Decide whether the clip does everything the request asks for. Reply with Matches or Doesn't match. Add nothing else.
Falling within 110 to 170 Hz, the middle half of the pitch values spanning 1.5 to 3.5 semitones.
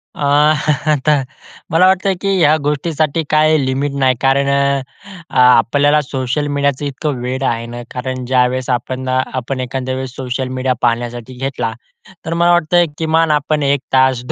Matches